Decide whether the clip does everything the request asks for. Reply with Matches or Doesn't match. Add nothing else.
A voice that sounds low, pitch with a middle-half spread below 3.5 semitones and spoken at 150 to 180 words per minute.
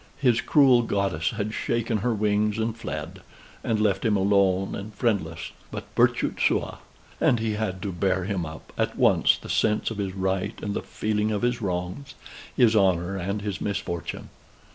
Matches